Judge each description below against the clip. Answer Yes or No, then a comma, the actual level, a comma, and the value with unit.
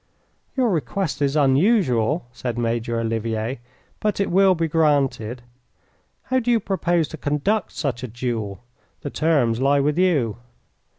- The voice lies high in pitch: No, medium, 140 Hz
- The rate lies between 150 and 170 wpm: No, average, 140 wpm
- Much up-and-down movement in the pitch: Yes, wide, 6.7 semitones